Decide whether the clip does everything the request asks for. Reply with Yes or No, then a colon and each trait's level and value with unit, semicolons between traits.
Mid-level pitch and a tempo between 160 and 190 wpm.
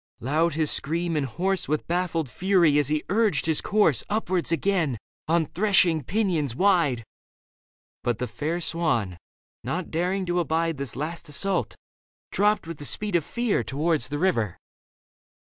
No: medium, 165 Hz; average, 150 wpm